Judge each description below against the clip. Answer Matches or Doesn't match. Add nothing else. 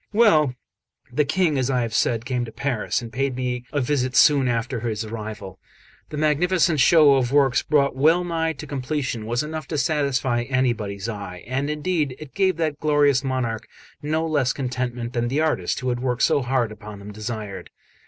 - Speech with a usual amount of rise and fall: Matches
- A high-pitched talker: Doesn't match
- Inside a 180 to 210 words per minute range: Matches